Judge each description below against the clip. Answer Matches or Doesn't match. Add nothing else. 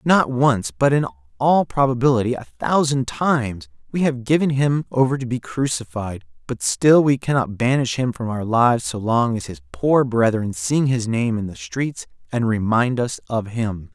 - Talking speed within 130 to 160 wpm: Doesn't match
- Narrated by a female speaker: Doesn't match